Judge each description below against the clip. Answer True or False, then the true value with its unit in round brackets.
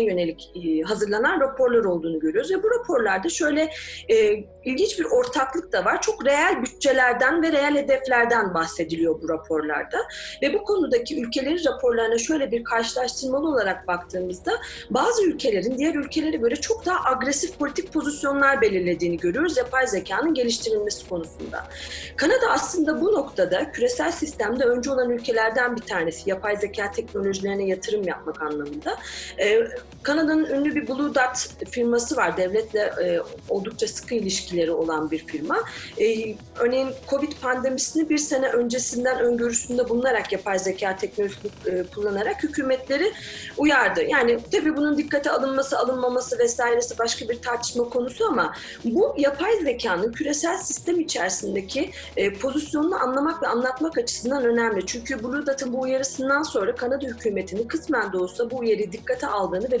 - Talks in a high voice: True (260 Hz)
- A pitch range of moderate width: False (5.9 semitones)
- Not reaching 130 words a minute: False (140 wpm)